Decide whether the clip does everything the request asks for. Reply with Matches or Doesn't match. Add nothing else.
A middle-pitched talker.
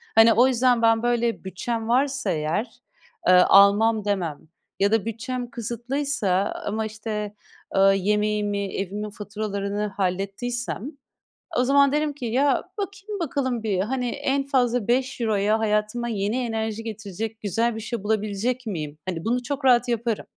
Doesn't match